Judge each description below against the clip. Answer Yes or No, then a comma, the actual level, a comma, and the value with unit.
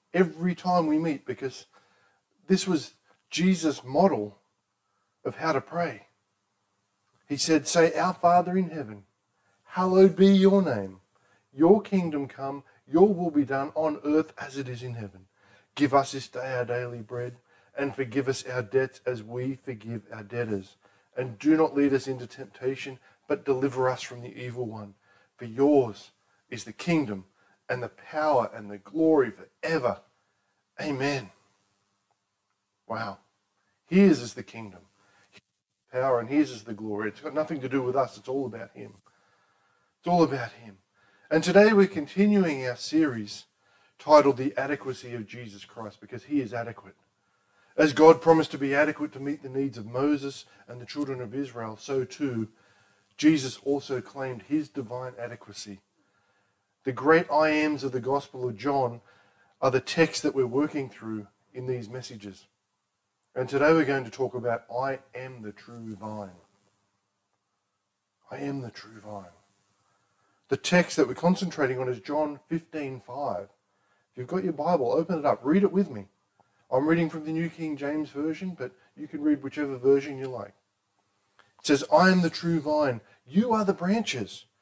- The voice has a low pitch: Yes, low, 125 Hz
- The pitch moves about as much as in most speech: No, wide, 6.4 semitones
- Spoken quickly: No, average, 165 wpm